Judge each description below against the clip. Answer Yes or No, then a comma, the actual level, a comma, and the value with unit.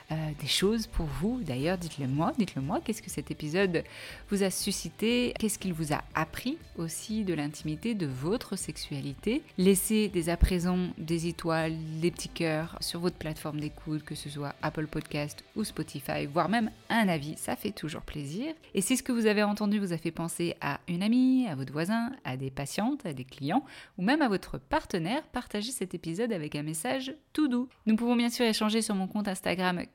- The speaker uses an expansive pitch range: Yes, wide, 5.9 semitones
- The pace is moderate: Yes, average, 200 wpm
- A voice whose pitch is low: No, medium, 180 Hz